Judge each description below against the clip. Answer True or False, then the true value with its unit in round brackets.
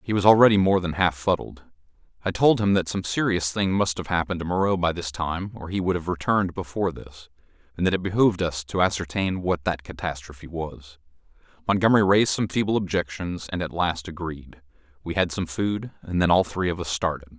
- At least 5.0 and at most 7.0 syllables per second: True (5.8 syllables/s)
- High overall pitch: False (90 Hz)